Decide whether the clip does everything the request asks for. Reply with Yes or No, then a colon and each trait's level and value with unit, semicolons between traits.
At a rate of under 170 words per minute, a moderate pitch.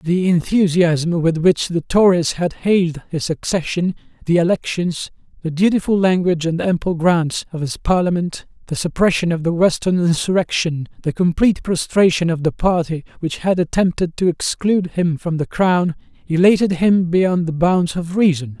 Yes: average, 160 wpm; medium, 175 Hz